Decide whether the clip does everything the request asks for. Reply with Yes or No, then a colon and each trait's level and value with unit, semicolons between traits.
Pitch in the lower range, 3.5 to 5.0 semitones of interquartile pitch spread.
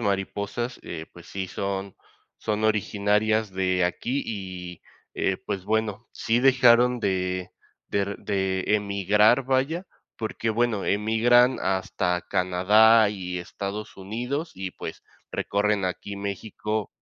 No: low, 100 Hz; average, 2.9 semitones